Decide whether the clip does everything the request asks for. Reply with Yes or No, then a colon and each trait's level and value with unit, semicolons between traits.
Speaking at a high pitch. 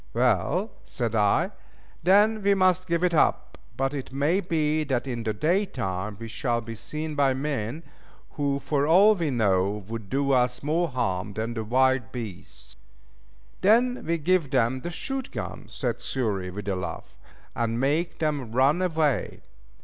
No: low, 135 Hz